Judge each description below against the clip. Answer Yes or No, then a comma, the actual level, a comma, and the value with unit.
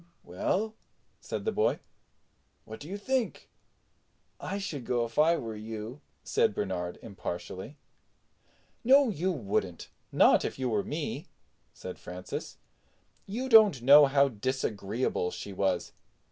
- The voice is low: Yes, low, 130 Hz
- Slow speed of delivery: Yes, slow, 130 wpm